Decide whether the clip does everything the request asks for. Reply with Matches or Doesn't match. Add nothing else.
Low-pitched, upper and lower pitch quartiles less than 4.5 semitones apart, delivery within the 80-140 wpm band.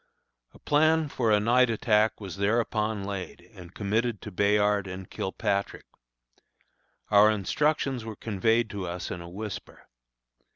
Matches